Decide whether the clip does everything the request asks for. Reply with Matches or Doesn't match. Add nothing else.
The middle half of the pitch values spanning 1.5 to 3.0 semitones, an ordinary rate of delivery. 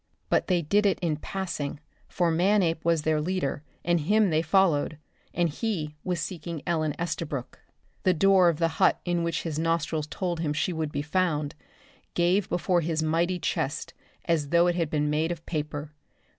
Matches